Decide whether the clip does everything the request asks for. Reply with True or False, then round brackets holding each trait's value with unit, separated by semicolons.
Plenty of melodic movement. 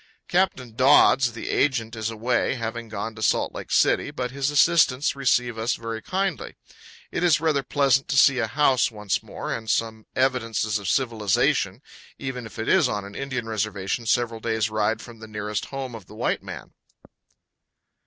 False (3.3 semitones)